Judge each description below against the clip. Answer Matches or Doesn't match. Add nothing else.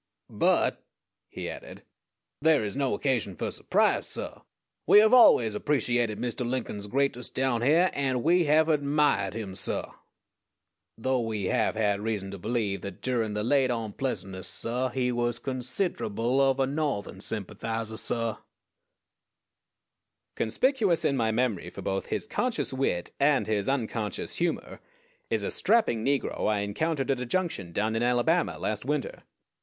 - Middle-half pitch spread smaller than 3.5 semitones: Doesn't match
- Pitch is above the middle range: Doesn't match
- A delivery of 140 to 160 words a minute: Matches